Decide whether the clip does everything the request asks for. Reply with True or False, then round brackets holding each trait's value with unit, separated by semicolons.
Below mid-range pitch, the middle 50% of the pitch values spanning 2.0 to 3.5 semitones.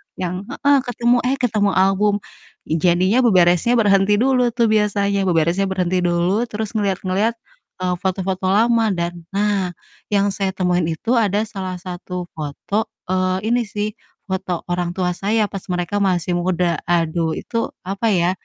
False (190 Hz; 2.8 semitones)